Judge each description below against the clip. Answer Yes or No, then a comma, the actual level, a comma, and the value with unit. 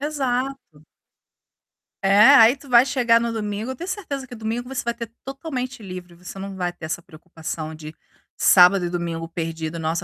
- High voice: Yes, high, 210 Hz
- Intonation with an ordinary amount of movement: No, wide, 6.8 semitones